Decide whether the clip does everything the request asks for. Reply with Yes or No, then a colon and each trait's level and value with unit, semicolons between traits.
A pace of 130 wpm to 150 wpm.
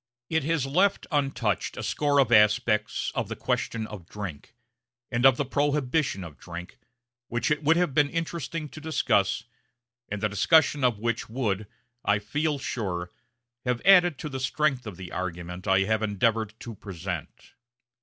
No: average, 165 wpm